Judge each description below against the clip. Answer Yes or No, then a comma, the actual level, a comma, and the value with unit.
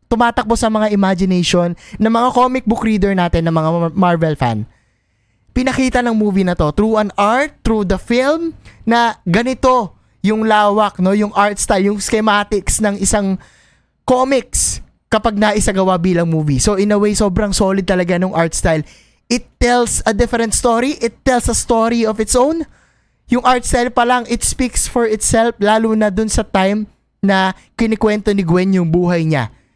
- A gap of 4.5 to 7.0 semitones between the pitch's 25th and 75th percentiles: No, average, 4.0 semitones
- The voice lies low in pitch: No, high, 210 Hz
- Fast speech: Yes, fast, 175 wpm